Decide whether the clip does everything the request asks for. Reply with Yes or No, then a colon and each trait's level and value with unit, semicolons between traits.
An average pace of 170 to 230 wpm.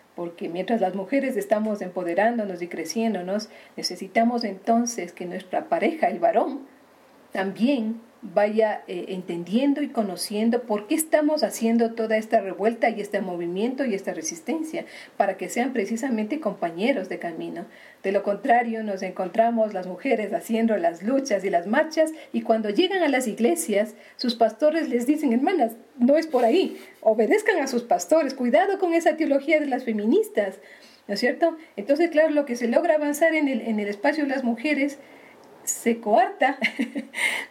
No: average, 160 wpm